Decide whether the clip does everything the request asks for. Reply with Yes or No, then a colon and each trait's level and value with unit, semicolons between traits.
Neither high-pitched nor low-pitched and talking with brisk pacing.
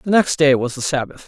Yes: medium, 145 Hz; fast, 285 wpm